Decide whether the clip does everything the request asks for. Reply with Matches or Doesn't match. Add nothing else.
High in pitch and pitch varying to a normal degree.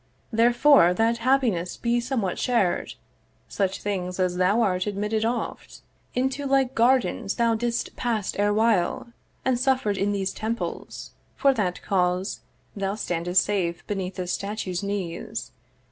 Matches